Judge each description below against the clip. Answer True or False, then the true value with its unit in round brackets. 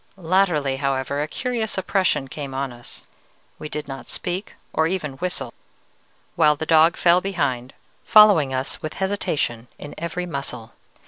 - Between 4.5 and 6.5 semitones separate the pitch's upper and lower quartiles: True (5.1 semitones)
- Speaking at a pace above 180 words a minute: False (145 wpm)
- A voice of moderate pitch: True (155 Hz)